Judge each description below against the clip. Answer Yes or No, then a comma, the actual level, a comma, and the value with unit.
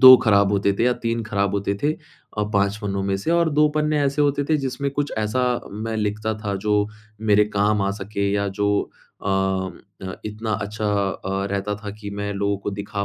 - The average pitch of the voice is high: No, low, 105 Hz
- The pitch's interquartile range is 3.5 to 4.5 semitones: No, average, 2.9 semitones